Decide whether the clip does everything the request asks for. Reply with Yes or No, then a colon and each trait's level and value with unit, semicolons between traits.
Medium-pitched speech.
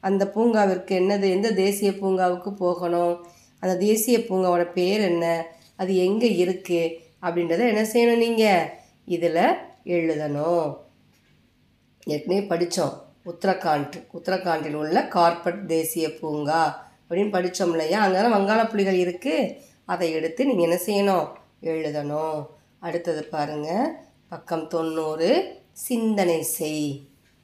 Yes: medium, 175 Hz